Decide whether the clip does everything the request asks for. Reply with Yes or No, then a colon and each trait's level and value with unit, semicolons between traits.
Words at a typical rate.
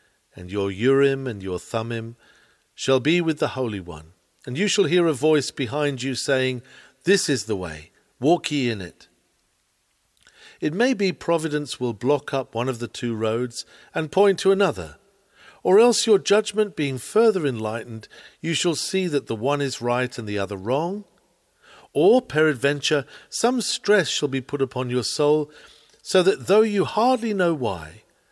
Yes: average, 170 wpm